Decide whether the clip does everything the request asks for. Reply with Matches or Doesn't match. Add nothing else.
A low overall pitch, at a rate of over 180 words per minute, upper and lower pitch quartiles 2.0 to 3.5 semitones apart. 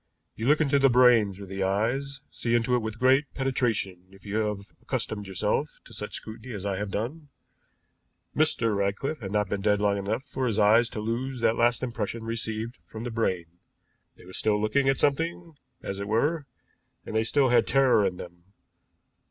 Doesn't match